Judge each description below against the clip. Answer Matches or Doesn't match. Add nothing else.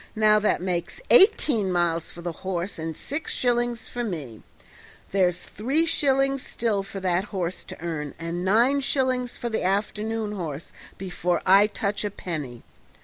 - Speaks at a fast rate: Doesn't match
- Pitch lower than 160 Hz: Doesn't match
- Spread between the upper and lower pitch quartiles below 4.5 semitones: Doesn't match